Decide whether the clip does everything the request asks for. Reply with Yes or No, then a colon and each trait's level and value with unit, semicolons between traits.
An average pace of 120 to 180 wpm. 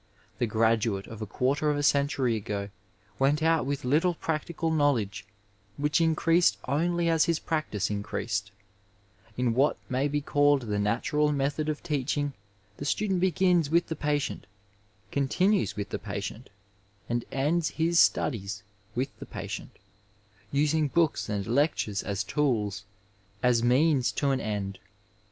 Yes: average, 145 wpm